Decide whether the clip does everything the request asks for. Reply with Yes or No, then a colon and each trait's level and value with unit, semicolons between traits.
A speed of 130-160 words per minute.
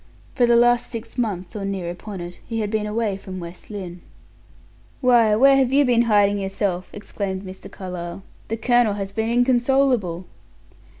No: average, 170 wpm